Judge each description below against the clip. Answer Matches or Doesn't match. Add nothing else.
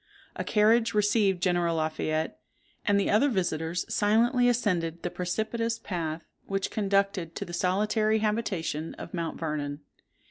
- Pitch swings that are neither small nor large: Matches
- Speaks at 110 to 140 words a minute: Matches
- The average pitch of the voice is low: Doesn't match